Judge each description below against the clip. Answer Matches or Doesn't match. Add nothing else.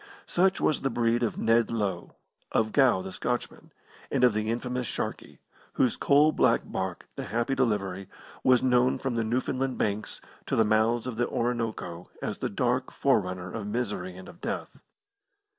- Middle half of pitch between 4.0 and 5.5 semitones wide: Doesn't match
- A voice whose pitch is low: Matches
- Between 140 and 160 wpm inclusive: Doesn't match